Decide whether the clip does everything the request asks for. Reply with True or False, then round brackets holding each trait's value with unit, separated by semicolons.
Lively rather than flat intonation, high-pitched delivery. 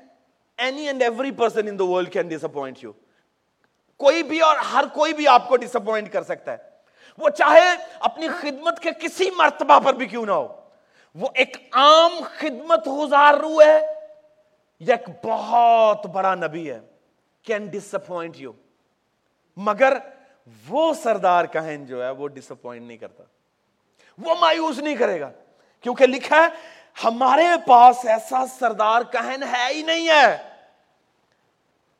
True (6.3 semitones; 265 Hz)